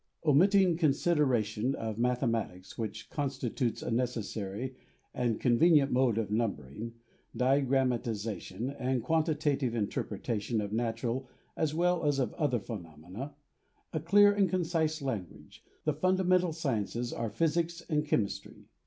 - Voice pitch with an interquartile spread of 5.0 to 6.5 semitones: Yes, wide, 5.5 semitones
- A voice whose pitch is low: Yes, low, 130 Hz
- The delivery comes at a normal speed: No, slow, 125 wpm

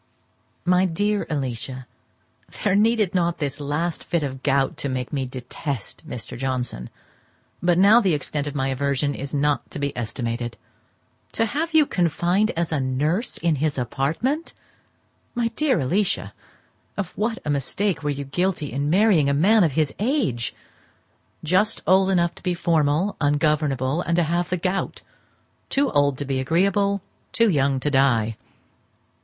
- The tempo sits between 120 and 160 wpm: Yes, average, 155 wpm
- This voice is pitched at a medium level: Yes, medium, 155 Hz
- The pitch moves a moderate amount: No, wide, 5.8 semitones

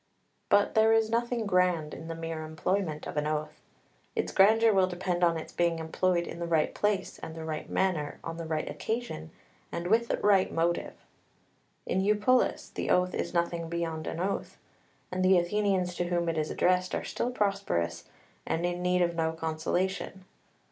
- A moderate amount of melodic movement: Yes, average, 3.1 semitones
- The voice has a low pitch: No, medium, 175 Hz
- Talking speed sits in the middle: Yes, average, 180 wpm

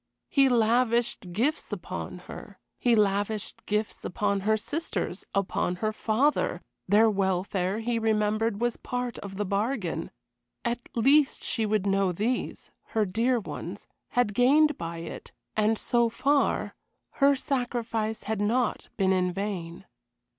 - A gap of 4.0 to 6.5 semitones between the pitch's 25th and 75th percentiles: No, average, 3.5 semitones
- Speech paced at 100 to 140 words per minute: Yes, slow, 135 wpm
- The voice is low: No, high, 220 Hz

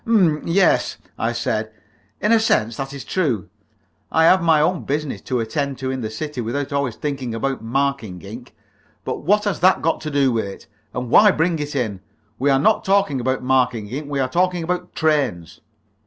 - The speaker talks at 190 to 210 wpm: Yes, average, 200 wpm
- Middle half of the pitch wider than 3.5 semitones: Yes, average, 4.7 semitones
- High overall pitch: No, medium, 140 Hz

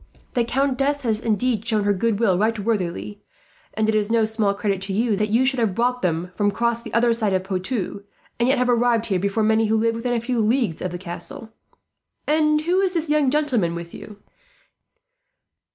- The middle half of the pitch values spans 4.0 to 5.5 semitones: No, average, 3.5 semitones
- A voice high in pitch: Yes, high, 225 Hz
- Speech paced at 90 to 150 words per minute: No, fast, 205 wpm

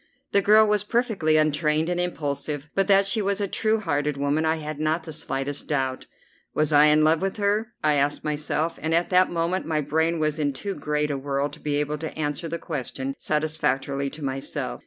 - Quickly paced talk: Yes, fast, 210 wpm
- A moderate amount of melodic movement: Yes, average, 3.2 semitones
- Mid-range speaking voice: Yes, medium, 155 Hz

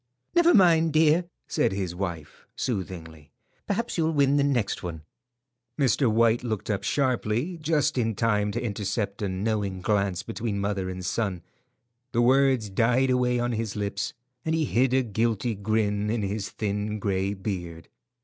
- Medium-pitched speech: No, low, 110 Hz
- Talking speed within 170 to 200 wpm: No, average, 160 wpm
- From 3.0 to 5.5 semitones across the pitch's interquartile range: Yes, average, 4.5 semitones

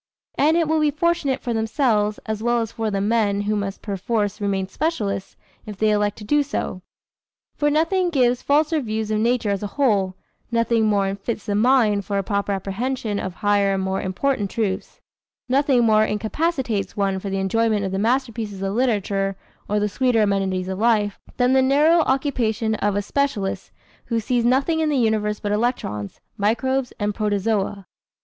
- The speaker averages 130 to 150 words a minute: No, average, 180 wpm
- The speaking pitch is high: Yes, high, 215 Hz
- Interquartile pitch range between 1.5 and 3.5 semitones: No, average, 4.2 semitones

